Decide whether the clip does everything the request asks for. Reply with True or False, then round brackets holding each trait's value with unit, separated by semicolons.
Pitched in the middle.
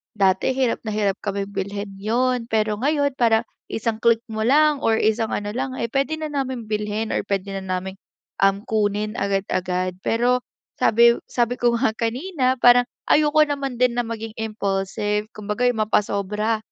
False (220 Hz)